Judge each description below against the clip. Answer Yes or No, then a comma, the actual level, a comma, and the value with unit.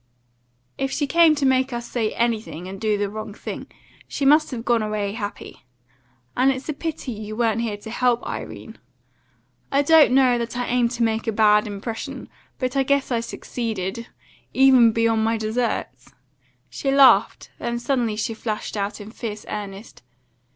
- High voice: Yes, high, 230 Hz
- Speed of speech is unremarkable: Yes, average, 170 wpm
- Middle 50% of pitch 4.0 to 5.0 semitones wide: No, average, 3.2 semitones